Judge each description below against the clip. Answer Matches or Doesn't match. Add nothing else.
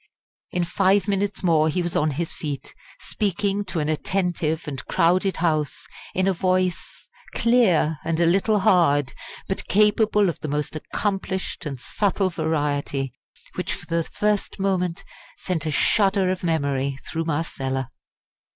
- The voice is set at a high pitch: Doesn't match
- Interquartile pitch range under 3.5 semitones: Doesn't match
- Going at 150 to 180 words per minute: Doesn't match